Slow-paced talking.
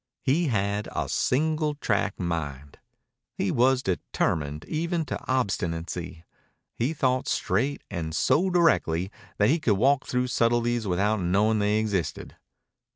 Yes: slow, 130 wpm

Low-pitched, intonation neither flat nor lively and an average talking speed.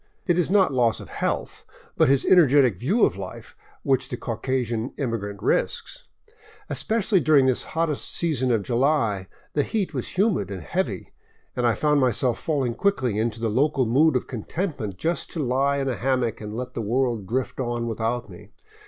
Yes: low, 130 Hz; average, 4.6 semitones; average, 180 wpm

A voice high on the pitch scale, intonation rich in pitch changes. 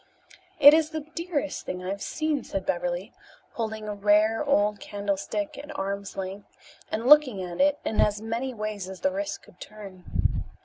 Yes: high, 215 Hz; wide, 6.3 semitones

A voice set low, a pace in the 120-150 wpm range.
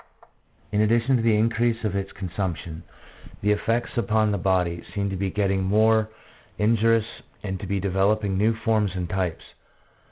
No: low, 105 Hz; average, 165 wpm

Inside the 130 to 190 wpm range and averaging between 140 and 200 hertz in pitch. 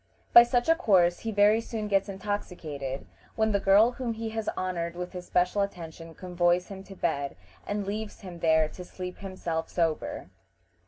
Yes: average, 175 wpm; medium, 185 Hz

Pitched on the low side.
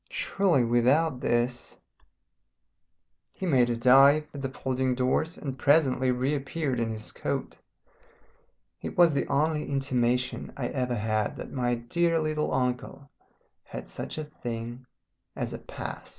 Yes: low, 130 Hz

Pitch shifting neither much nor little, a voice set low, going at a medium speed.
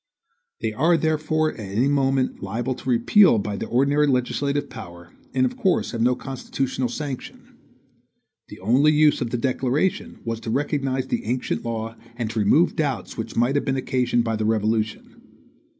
Yes: average, 4.1 semitones; low, 130 Hz; average, 170 wpm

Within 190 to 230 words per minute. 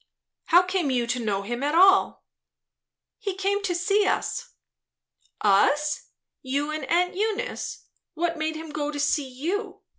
No: average, 150 wpm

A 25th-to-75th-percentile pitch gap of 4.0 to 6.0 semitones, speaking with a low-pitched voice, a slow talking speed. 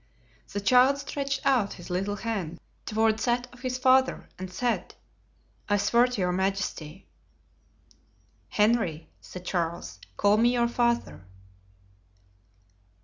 No: average, 4.9 semitones; high, 220 Hz; slow, 120 wpm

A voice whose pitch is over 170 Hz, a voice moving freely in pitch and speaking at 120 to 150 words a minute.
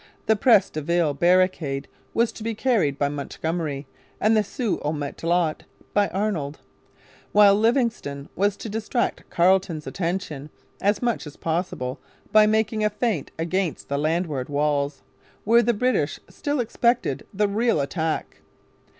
Yes: medium, 185 Hz; wide, 6.3 semitones; average, 140 wpm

